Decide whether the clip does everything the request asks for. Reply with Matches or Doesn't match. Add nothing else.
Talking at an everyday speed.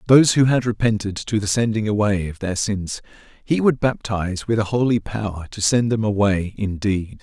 Matches